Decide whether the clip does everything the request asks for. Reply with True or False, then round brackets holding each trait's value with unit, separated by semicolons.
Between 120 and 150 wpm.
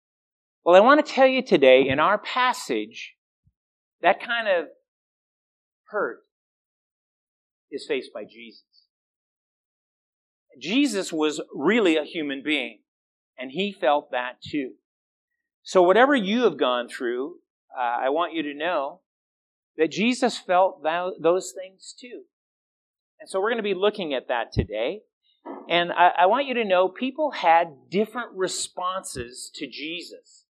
True (135 wpm)